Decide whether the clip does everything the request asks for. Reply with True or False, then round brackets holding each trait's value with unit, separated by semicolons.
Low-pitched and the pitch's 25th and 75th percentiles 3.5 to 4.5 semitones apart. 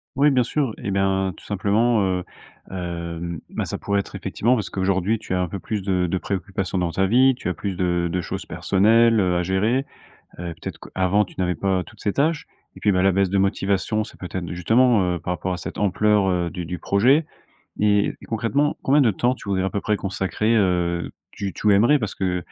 False (95 Hz; 3.1 semitones)